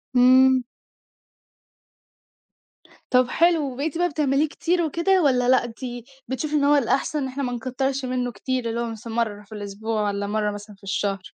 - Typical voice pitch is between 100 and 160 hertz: No, very high, 250 Hz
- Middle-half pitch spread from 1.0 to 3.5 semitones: No, average, 4.1 semitones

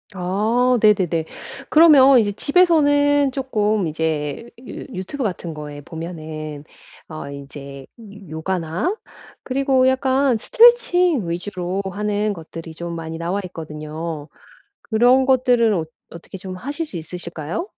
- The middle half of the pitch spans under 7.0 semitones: No, wide, 8.2 semitones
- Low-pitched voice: No, high, 195 Hz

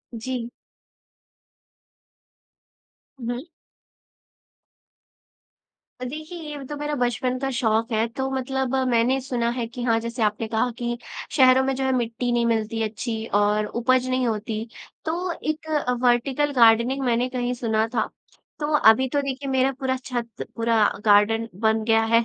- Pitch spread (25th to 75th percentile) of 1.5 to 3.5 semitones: Yes, average, 2.7 semitones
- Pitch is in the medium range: No, high, 240 Hz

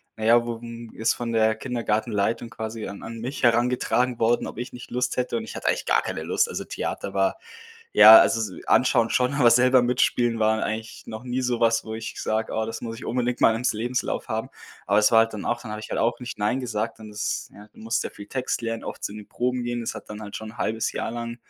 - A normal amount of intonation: No, narrow, 1.9 semitones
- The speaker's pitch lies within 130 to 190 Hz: No, low, 115 Hz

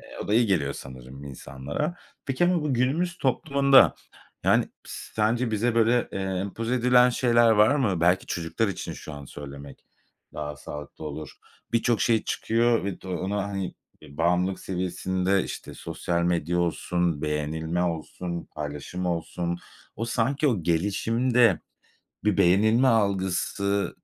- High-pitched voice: No, very low, 95 Hz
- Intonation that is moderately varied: No, wide, 5.8 semitones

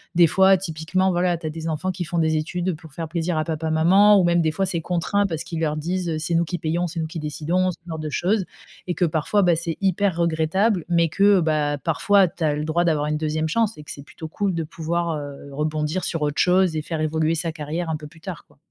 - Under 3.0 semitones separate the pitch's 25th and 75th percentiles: Yes, narrow, 2.4 semitones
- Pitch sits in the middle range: Yes, medium, 165 Hz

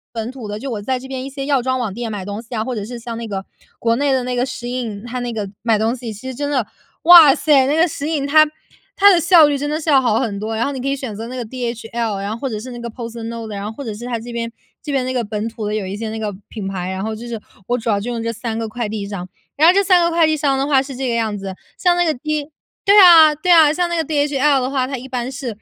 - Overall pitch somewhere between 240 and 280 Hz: Yes, high, 245 Hz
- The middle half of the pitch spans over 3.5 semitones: Yes, average, 4.2 semitones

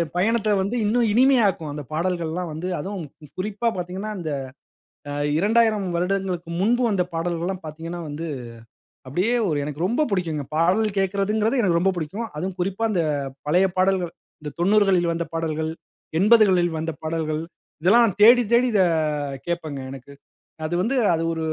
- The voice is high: No, medium, 180 Hz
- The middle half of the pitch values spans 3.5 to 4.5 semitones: Yes, average, 4.2 semitones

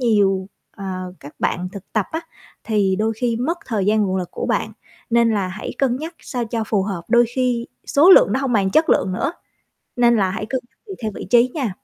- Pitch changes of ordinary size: Yes, average, 4.3 semitones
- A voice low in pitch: No, high, 225 Hz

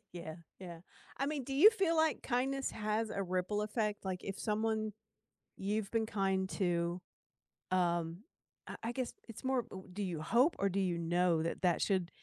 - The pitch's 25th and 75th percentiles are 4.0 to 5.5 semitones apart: Yes, average, 4.4 semitones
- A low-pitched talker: No, high, 200 Hz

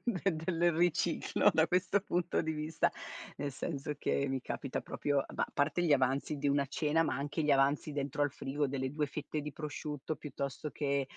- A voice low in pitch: No, medium, 145 Hz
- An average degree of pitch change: No, narrow, 2.2 semitones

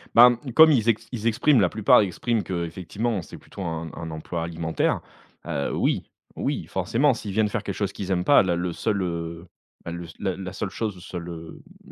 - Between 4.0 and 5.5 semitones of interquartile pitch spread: Yes, average, 4.5 semitones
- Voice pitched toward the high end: No, very low, 95 Hz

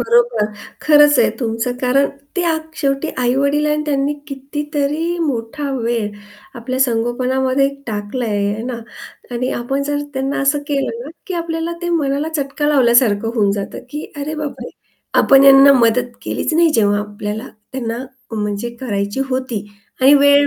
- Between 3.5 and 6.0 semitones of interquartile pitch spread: Yes, average, 3.8 semitones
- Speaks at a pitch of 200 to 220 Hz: No, very high, 265 Hz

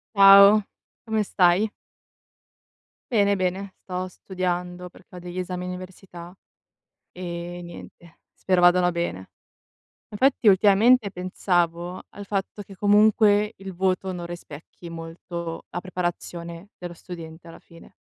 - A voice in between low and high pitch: Yes, medium, 180 Hz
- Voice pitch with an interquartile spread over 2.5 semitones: No, narrow, 2.2 semitones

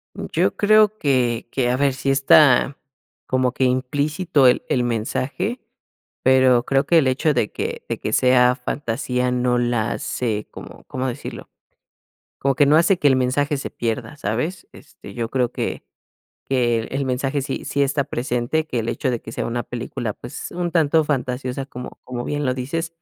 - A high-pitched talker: No, low, 130 Hz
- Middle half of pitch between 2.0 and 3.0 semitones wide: Yes, average, 2.7 semitones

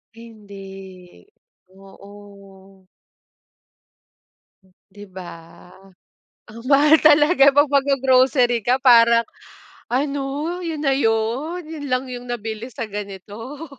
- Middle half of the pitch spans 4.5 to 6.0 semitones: Yes, wide, 5.6 semitones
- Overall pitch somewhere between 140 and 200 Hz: No, high, 235 Hz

